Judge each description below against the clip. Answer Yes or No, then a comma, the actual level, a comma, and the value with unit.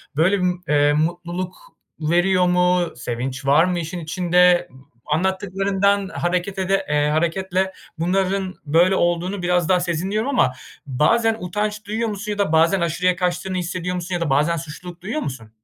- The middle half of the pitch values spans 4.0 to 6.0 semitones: No, narrow, 2.5 semitones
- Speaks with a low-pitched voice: No, medium, 180 Hz